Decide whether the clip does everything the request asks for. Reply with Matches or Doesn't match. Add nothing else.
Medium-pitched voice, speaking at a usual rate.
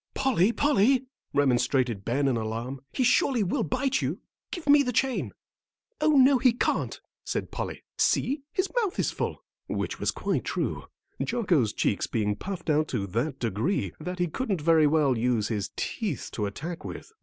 Matches